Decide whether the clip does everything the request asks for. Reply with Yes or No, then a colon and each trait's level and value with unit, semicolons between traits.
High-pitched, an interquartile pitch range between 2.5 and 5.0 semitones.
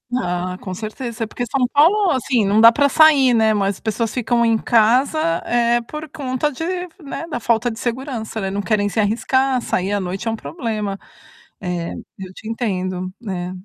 Yes: high, 230 Hz; average, 4.1 semitones